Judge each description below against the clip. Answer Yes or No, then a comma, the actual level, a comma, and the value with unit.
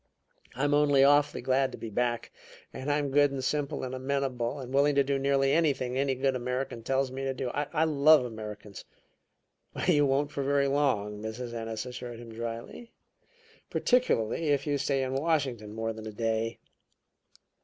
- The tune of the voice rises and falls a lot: No, average, 3.3 semitones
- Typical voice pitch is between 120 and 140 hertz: Yes, low, 135 Hz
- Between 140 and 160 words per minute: No, average, 170 wpm